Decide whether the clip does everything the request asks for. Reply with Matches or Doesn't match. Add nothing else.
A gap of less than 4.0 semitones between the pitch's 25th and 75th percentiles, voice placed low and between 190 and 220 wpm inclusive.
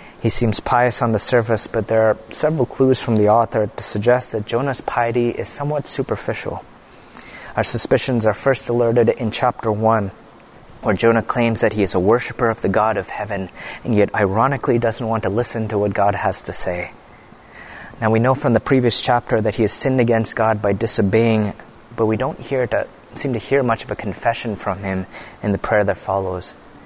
Matches